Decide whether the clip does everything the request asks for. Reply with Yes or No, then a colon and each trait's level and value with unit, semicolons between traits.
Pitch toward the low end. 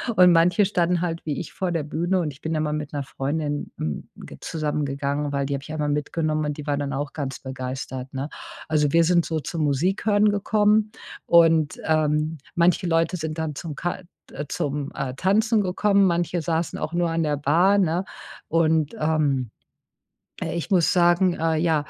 No: medium, 160 Hz